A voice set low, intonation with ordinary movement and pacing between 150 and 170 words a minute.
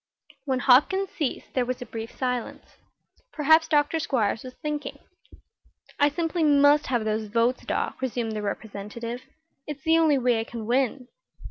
No: very high, 255 Hz; average, 4.2 semitones; average, 155 wpm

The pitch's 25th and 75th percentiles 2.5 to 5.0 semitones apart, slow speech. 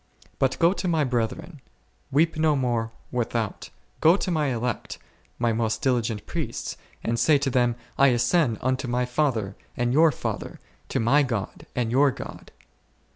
No: average, 4.1 semitones; average, 160 wpm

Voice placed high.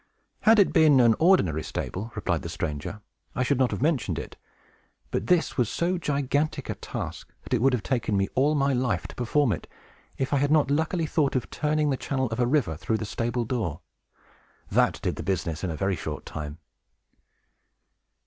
No: low, 125 Hz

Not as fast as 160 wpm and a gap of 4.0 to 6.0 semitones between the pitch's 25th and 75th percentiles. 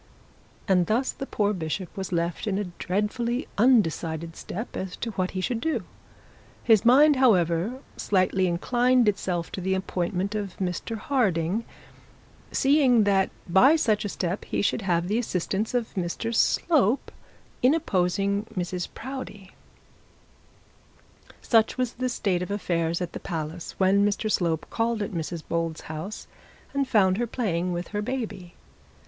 Yes: average, 150 wpm; average, 4.6 semitones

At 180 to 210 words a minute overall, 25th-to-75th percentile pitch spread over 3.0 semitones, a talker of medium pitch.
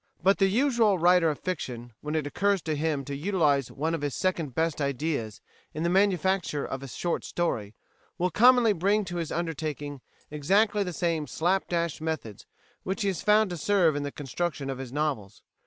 Yes: average, 190 wpm; average, 4.6 semitones; medium, 165 Hz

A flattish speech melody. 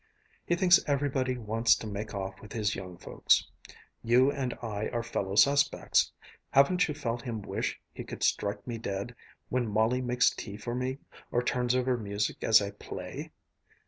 No: average, 3.5 semitones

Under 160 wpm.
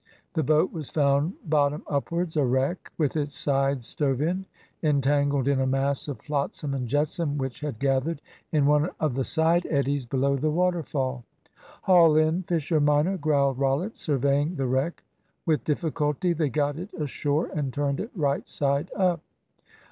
No: average, 165 wpm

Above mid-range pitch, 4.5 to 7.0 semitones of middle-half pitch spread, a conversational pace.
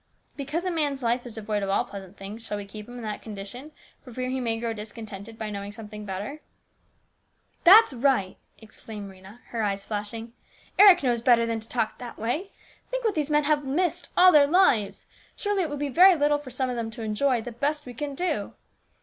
No: high, 235 Hz; wide, 5.6 semitones; fast, 230 wpm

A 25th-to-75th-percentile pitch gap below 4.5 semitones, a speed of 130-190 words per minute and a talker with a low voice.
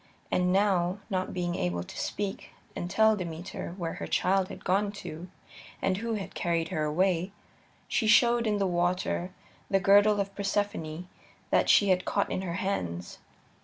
No: narrow, 2.6 semitones; average, 165 wpm; medium, 185 Hz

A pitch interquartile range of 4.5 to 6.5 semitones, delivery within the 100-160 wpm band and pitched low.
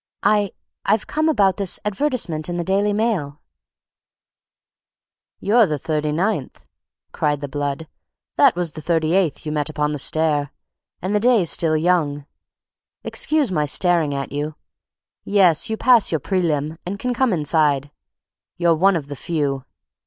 No: average, 5.3 semitones; average, 150 wpm; medium, 165 Hz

